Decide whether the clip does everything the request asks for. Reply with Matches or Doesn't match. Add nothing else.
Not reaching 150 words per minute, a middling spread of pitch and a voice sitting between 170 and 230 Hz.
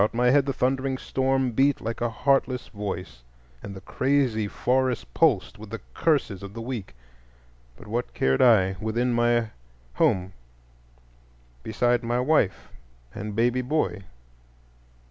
Doesn't match